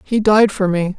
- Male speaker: No, female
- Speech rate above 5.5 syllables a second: No, 4.5 syllables/s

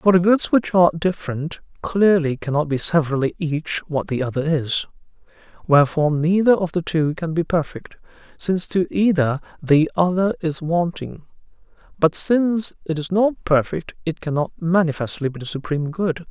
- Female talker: No, male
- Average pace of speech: Yes, average, 160 wpm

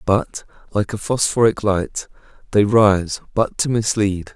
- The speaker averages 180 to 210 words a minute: No, average, 140 wpm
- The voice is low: Yes, low, 105 Hz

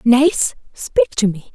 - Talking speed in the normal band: Yes, average, 155 wpm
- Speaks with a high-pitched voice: Yes, high, 220 Hz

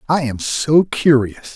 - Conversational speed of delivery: Yes, average, 155 wpm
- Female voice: No, male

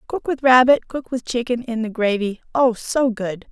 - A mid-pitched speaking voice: No, high, 240 Hz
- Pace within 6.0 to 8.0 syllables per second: No, 4.7 syllables/s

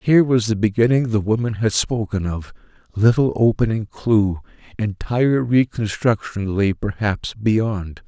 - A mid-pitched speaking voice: No, low, 110 Hz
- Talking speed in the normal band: No, slow, 120 wpm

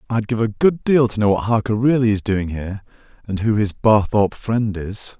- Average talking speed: No, fast, 210 wpm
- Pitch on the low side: Yes, low, 110 Hz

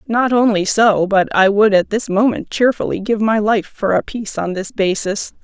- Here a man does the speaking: No, female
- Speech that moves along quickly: Yes, fast, 210 wpm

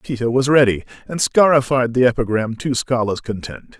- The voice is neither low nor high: No, low, 125 Hz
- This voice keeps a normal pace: Yes, average, 160 wpm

